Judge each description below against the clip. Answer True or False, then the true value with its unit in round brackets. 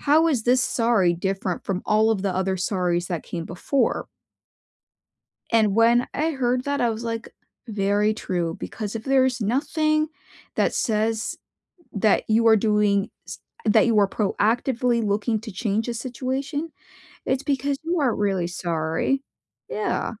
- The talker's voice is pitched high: True (225 Hz)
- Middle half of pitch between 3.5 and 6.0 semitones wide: True (4.3 semitones)